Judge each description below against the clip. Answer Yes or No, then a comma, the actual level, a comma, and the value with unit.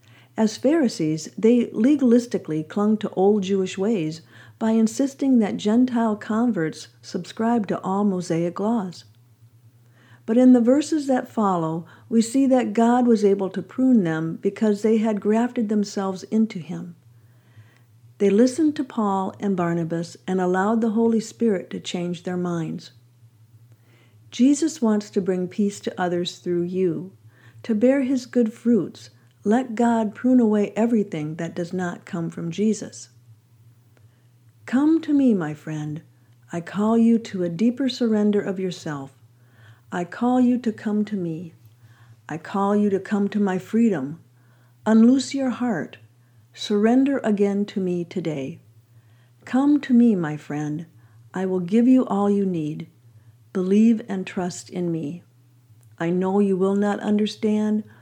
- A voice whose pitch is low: No, high, 190 Hz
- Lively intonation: Yes, wide, 7.2 semitones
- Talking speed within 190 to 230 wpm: No, average, 145 wpm